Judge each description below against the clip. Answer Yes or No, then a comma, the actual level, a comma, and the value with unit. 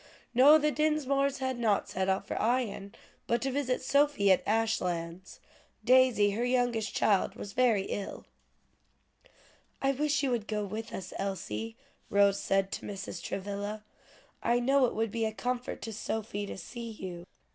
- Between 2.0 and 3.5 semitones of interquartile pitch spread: No, average, 4.3 semitones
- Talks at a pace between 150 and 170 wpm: Yes, average, 160 wpm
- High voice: Yes, high, 225 Hz